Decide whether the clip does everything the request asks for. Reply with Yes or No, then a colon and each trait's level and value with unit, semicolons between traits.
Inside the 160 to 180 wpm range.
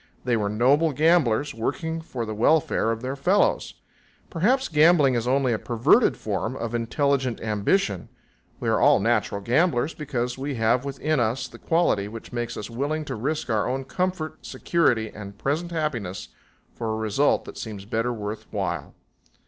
Yes: average, 165 wpm